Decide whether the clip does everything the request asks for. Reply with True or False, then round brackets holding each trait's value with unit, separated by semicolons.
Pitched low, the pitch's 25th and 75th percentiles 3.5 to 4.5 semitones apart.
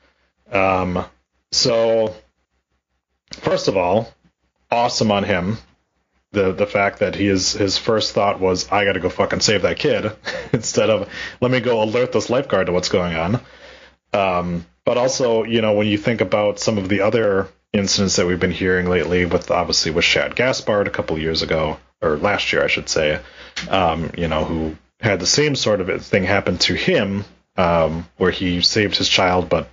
True (95 Hz; 4.0 semitones)